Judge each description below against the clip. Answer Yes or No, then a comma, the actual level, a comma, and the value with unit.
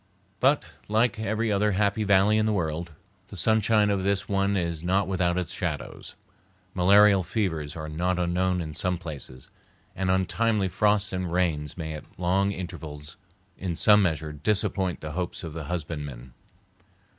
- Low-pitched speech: Yes, very low, 90 Hz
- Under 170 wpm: Yes, average, 155 wpm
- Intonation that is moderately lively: Yes, average, 3.7 semitones